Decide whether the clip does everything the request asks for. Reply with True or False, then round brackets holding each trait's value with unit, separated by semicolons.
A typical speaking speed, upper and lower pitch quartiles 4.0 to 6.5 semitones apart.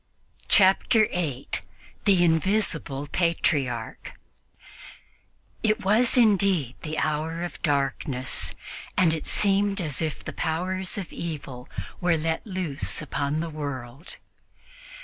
False (110 wpm; 4.5 semitones)